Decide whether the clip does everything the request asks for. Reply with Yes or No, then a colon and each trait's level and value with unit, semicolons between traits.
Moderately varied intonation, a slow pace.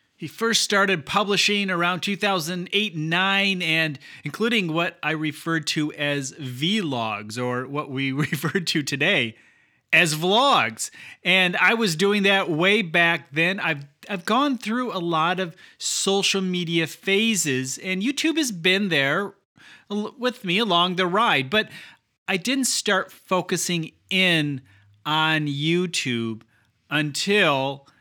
Yes: average, 4.9 semitones; slow, 130 wpm